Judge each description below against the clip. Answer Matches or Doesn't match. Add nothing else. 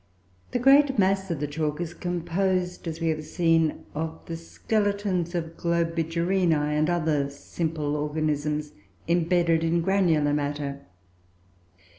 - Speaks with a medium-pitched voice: Matches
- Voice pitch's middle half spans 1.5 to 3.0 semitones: Matches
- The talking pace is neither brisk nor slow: Doesn't match